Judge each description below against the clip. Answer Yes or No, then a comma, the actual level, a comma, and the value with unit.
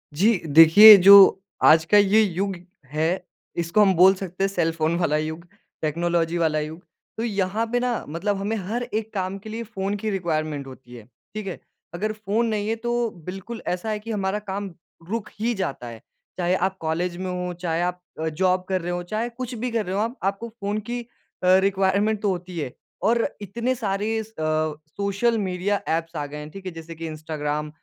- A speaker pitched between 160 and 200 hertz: Yes, high, 190 Hz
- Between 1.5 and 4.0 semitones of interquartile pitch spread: No, average, 4.4 semitones